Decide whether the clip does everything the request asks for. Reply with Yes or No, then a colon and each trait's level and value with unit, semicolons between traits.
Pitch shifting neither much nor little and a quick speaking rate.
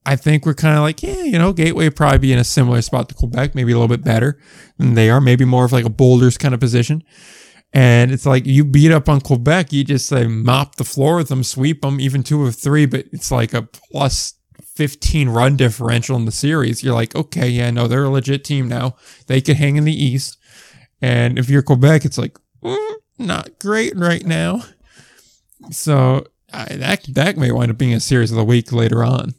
Yes: average, 3.5 semitones; fast, 230 wpm